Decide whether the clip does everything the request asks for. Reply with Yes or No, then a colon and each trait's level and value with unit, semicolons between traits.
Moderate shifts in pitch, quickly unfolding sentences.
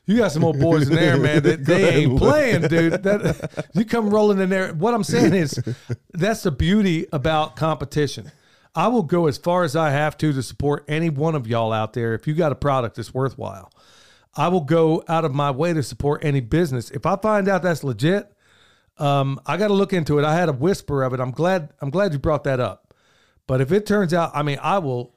Yes: average, 4.2 semitones; fast, 235 wpm